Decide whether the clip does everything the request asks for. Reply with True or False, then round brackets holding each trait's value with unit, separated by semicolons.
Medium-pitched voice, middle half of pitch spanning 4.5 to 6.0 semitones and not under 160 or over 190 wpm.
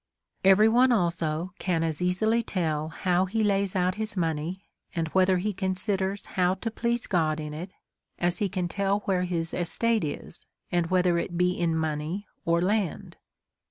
False (180 Hz; 3.0 semitones; 170 wpm)